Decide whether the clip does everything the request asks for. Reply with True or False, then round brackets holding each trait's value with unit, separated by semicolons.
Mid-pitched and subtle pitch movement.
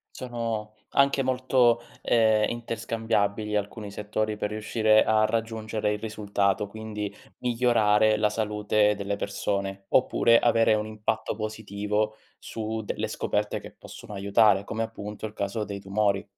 False (110 Hz; 1.3 semitones)